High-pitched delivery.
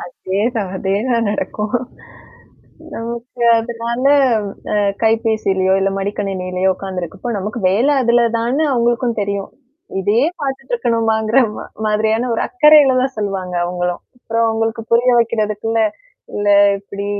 Yes: high, 225 Hz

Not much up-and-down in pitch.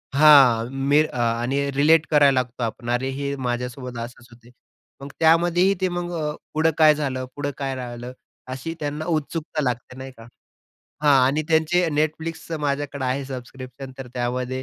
No: average, 3.4 semitones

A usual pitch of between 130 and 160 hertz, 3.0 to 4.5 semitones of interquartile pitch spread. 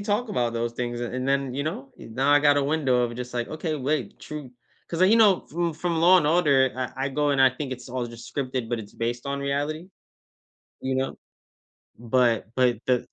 Yes: low, 135 Hz; average, 3.7 semitones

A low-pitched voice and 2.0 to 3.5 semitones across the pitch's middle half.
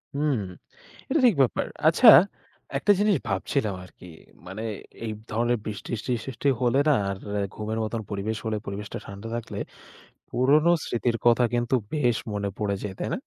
No: low, 115 Hz; average, 4.3 semitones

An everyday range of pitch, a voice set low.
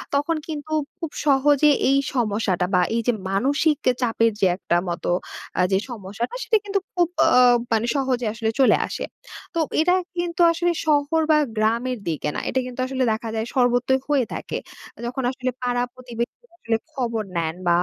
No: average, 4.4 semitones; very high, 250 Hz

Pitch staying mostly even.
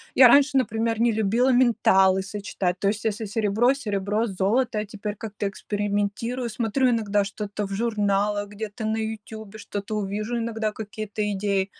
Yes: narrow, 2.1 semitones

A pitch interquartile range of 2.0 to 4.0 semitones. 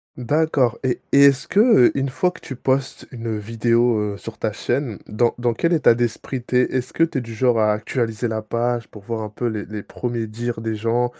Yes: average, 2.8 semitones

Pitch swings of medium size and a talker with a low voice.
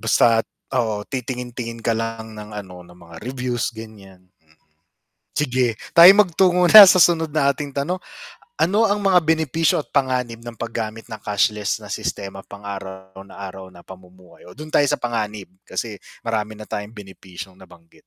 No: wide, 6.1 semitones; low, 115 Hz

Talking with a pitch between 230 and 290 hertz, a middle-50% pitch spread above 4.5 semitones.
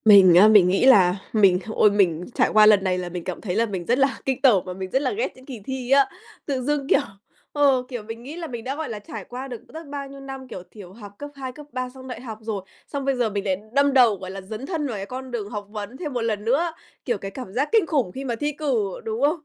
Yes: high, 240 Hz; average, 5.1 semitones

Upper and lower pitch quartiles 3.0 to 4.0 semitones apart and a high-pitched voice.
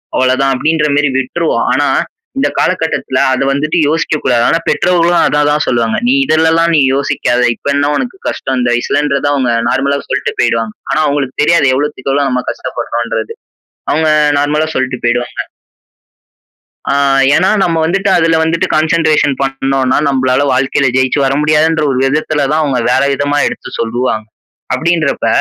No: average, 3.3 semitones; medium, 140 Hz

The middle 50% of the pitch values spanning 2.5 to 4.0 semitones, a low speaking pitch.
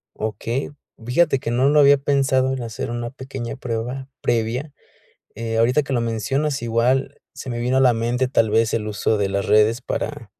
Yes: average, 2.8 semitones; low, 120 Hz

